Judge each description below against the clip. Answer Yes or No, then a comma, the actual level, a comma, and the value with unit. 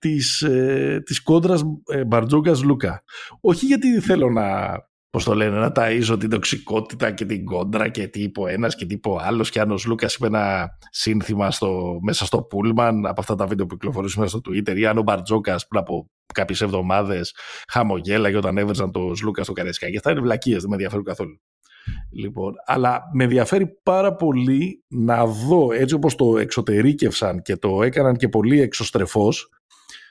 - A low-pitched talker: Yes, low, 110 Hz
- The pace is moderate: No, fast, 175 wpm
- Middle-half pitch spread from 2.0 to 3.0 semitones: No, average, 4.3 semitones